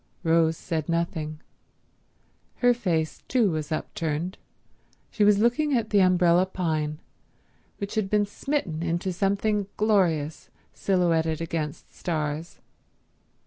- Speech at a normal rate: No, slow, 110 wpm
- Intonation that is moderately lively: Yes, average, 4.2 semitones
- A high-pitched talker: No, medium, 175 Hz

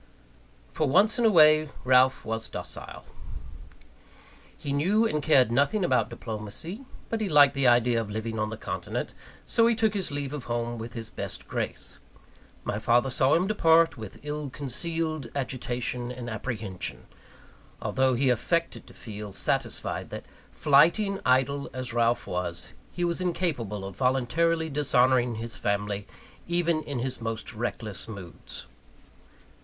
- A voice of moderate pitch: No, low, 130 Hz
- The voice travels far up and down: Yes, wide, 5.8 semitones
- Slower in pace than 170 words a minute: Yes, average, 150 wpm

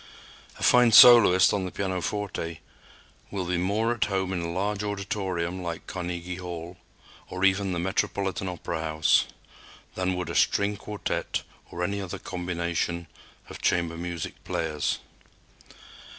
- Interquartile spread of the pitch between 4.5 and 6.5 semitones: No, narrow, 2.5 semitones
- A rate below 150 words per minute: Yes, slow, 135 wpm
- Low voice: Yes, very low, 90 Hz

